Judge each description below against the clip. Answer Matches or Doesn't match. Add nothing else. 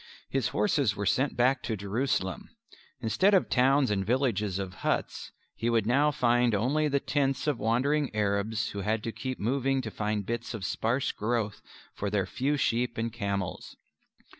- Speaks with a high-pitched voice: Doesn't match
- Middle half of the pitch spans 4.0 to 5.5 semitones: Matches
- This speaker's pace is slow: Doesn't match